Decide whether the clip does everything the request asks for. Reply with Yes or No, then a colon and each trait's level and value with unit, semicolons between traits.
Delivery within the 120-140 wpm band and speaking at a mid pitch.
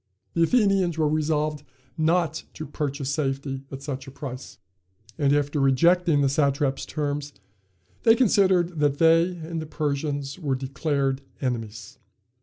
Yes: slow, 135 wpm; medium, 145 Hz